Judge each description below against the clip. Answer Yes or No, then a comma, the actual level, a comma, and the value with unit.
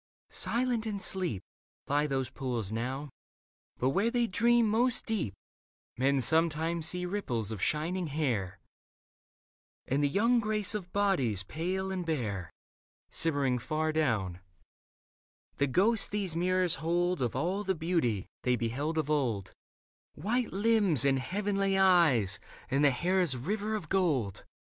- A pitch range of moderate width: No, wide, 7.0 semitones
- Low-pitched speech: No, medium, 160 Hz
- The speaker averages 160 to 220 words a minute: No, average, 140 wpm